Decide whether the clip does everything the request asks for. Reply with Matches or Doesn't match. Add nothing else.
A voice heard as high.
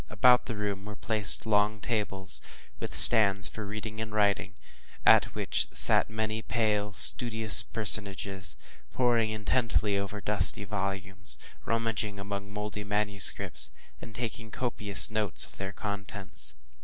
Doesn't match